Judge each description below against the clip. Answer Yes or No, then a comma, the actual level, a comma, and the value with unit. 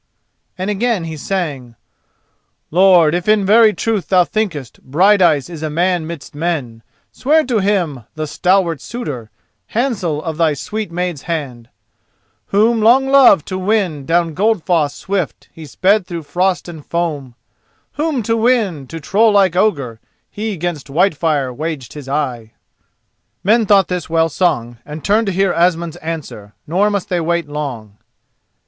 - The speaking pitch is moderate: Yes, medium, 175 Hz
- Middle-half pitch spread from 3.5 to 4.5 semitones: No, average, 5.0 semitones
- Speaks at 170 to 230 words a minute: No, average, 150 wpm